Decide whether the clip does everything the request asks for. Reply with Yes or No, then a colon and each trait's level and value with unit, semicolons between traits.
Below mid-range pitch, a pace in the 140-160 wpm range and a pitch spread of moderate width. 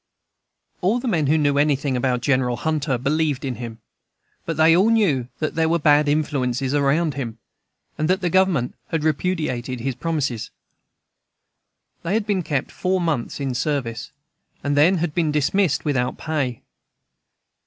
No: medium, 150 Hz; average, 155 wpm; average, 4.0 semitones